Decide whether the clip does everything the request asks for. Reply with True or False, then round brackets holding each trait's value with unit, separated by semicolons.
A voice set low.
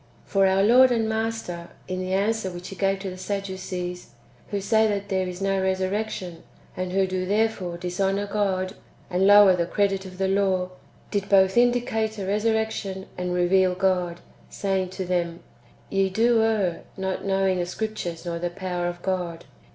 False (190 Hz)